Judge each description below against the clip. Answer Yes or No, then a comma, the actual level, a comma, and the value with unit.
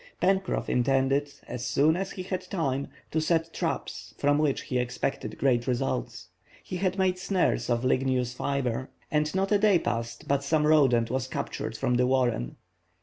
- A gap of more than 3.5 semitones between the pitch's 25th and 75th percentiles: Yes, average, 5.0 semitones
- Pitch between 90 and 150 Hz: Yes, medium, 140 Hz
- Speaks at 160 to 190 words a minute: Yes, average, 170 wpm